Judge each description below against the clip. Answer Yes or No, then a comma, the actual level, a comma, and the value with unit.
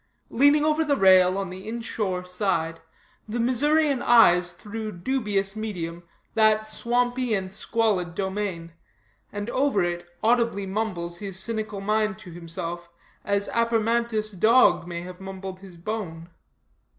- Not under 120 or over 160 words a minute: Yes, slow, 135 wpm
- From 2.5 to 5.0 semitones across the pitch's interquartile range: Yes, average, 4.1 semitones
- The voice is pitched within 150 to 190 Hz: No, high, 205 Hz